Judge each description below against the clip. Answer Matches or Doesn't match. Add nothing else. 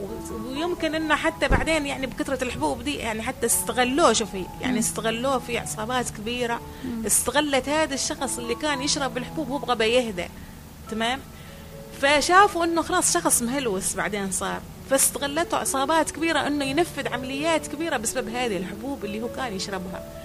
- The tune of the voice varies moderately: Matches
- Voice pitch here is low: Doesn't match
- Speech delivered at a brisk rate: Matches